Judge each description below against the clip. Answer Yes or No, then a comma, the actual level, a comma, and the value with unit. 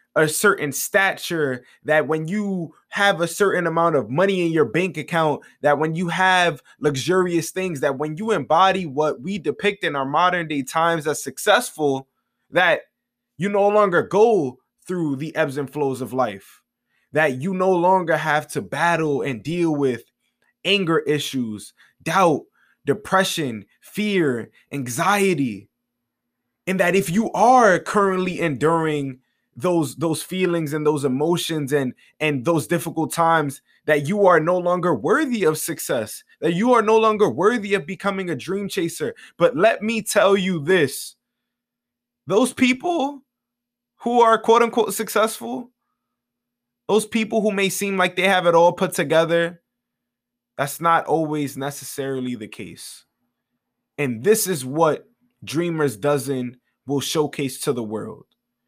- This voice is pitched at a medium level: Yes, medium, 165 Hz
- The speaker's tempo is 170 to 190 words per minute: No, average, 145 wpm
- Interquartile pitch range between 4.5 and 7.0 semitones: Yes, average, 5.1 semitones